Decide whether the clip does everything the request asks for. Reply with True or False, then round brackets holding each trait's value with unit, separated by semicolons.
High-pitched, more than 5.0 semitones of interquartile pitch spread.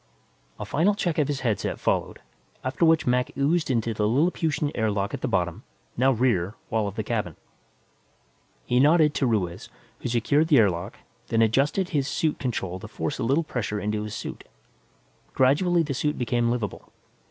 False (125 Hz; 5.6 semitones)